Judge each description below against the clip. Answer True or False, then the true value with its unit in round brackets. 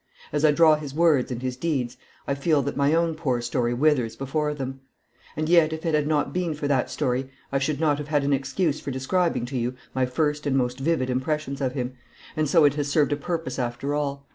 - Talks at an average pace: False (235 wpm)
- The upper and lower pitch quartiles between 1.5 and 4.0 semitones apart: True (2.9 semitones)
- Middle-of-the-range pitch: True (145 Hz)